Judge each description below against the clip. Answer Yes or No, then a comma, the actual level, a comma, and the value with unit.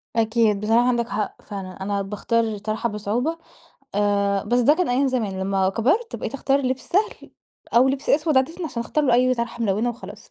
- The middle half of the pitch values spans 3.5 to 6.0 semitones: Yes, average, 4.1 semitones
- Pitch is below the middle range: No, high, 235 Hz